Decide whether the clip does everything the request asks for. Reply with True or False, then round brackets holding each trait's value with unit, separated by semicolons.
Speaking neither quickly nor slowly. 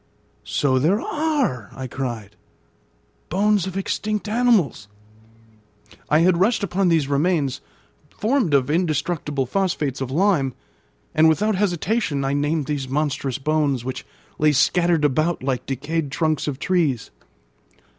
False (125 wpm)